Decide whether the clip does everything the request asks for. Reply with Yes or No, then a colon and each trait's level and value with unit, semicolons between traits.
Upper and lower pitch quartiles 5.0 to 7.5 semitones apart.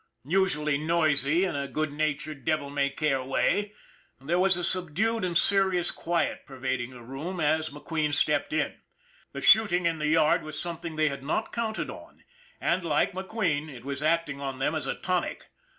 No: average, 3.8 semitones